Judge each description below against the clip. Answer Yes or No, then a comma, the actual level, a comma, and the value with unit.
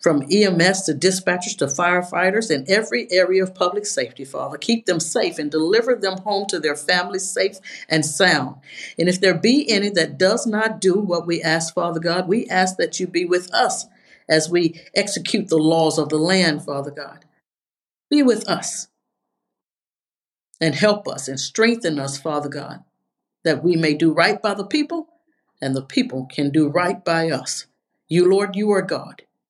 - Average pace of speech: Yes, average, 180 wpm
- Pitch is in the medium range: Yes, medium, 180 Hz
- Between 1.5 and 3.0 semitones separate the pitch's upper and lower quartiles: No, average, 4.3 semitones